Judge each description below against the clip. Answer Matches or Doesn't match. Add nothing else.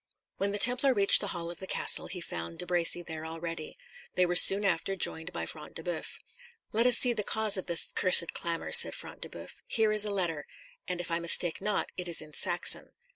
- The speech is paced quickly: Matches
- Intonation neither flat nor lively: Matches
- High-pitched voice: Doesn't match